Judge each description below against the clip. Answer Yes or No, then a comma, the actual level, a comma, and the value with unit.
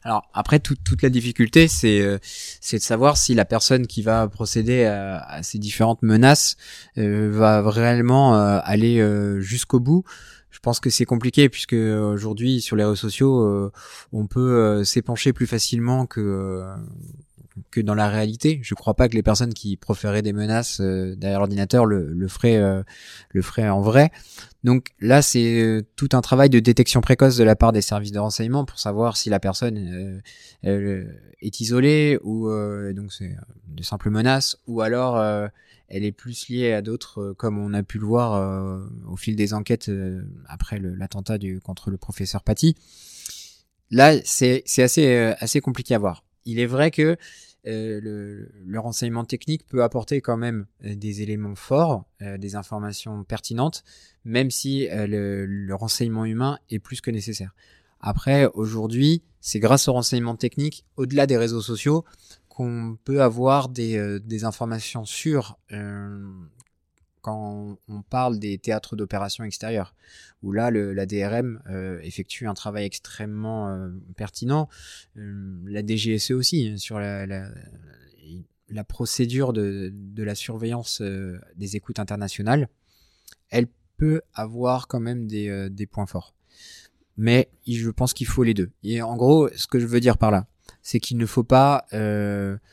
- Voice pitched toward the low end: Yes, low, 110 Hz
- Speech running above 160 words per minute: Yes, average, 170 wpm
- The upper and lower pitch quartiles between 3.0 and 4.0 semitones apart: Yes, average, 3.4 semitones